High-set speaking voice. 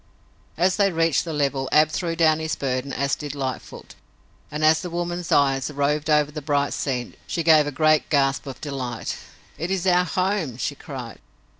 No: medium, 150 Hz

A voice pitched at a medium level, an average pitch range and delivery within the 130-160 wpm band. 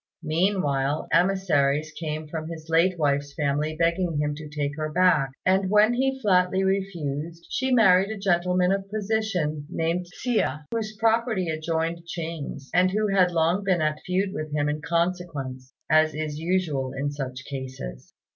Yes: medium, 165 Hz; average, 4.1 semitones; average, 155 wpm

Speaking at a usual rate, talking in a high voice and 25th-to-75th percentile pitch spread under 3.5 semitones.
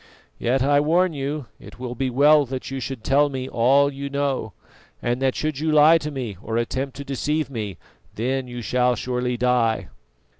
No: average, 190 wpm; low, 130 Hz; average, 2.7 semitones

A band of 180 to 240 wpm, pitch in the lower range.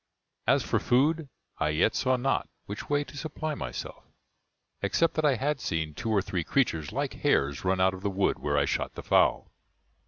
Yes: average, 195 wpm; low, 105 Hz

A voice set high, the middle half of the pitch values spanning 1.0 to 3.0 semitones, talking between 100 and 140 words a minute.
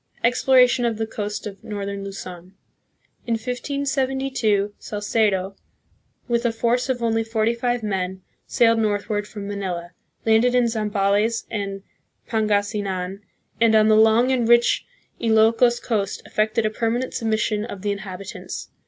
Yes: high, 220 Hz; average, 2.7 semitones; slow, 135 wpm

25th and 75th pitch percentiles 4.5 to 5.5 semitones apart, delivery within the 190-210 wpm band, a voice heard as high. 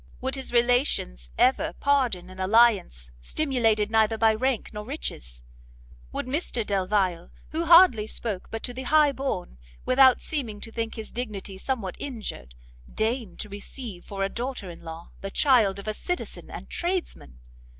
No: average, 5.1 semitones; average, 160 wpm; high, 225 Hz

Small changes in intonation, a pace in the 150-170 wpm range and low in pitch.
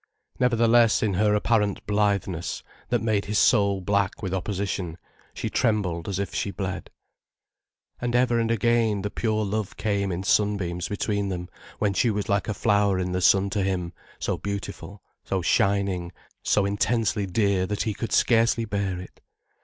Yes: narrow, 2.2 semitones; average, 165 wpm; low, 100 Hz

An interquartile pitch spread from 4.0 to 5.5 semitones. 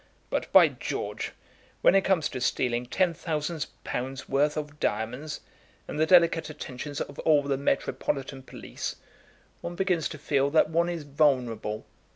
No: average, 3.5 semitones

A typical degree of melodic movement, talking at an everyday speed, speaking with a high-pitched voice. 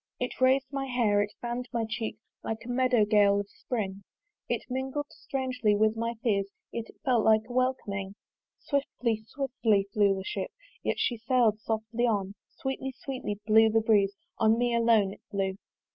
Yes: average, 3.3 semitones; average, 175 wpm; high, 225 Hz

